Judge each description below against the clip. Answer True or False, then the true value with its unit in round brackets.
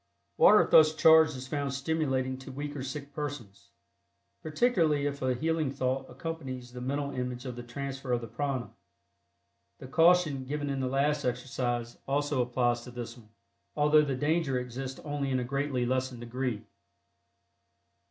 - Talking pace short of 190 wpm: True (160 wpm)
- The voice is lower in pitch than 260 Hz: True (135 Hz)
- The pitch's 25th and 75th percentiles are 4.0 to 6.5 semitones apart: False (2.7 semitones)